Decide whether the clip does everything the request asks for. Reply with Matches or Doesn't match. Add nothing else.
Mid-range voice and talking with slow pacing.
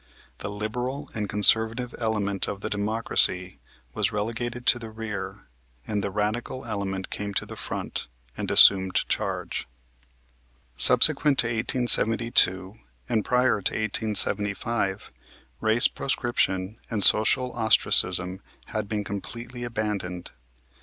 Doesn't match